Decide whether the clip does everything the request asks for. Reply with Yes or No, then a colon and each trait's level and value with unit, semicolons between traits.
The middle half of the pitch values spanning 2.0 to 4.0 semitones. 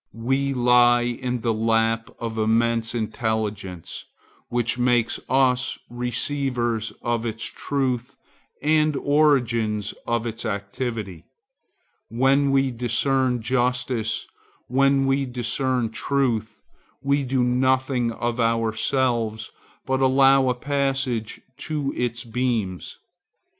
Yes: average, 2.7 semitones